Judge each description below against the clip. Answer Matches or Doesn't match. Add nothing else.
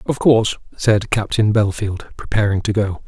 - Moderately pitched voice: Doesn't match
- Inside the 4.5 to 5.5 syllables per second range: Matches